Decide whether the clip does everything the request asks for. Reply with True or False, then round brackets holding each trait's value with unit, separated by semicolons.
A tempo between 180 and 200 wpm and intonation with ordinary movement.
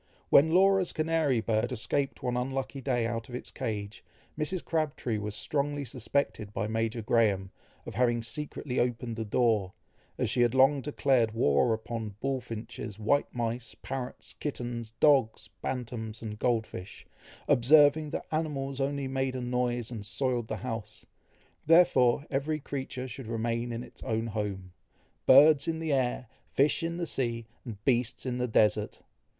False (155 wpm; 3.6 semitones)